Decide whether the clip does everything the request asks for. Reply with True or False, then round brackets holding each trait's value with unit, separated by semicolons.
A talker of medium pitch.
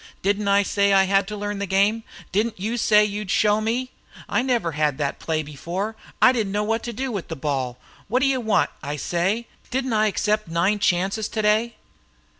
False (205 Hz)